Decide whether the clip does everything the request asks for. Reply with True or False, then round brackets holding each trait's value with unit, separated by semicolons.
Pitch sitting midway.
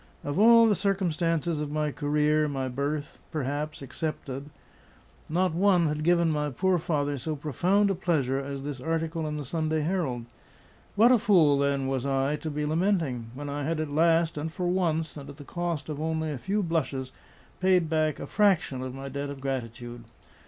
True (155 Hz)